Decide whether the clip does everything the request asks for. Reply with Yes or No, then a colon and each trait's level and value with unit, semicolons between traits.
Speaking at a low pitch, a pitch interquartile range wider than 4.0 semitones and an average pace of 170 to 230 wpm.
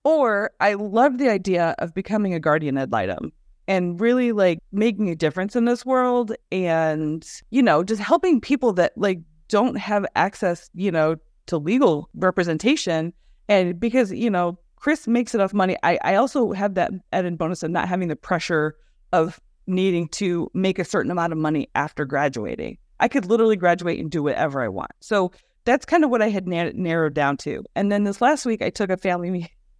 No: medium, 185 Hz; average, 5.3 semitones; average, 195 wpm